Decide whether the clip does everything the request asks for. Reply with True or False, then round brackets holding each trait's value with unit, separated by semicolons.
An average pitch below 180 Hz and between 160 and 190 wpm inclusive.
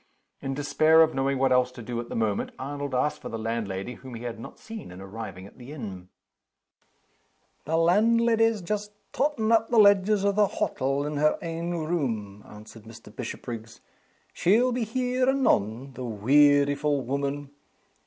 True (140 Hz; 165 wpm)